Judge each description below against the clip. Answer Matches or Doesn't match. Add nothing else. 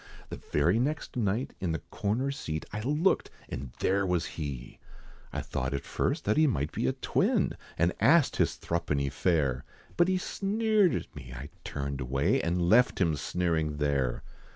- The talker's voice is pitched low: Matches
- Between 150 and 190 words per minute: Matches